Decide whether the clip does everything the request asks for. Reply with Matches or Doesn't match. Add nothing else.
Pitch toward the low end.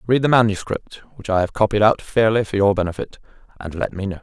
Matches